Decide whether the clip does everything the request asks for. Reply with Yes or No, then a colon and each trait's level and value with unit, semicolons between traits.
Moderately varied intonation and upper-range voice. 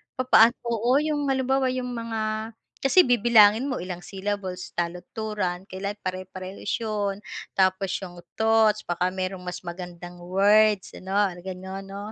Yes: average, 3.3 semitones; high, 200 Hz